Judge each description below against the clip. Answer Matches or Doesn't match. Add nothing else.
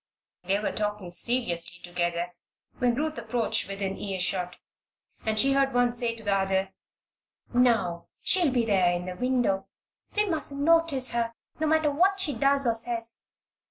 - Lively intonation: Matches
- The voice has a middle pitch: Doesn't match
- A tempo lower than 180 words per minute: Matches